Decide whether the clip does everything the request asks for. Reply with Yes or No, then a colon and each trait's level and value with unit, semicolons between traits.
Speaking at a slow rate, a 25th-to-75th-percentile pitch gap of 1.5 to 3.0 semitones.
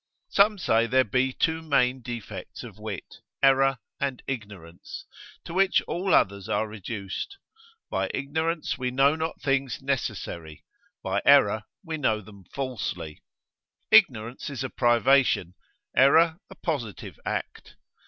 No: slow, 130 wpm; average, 4.9 semitones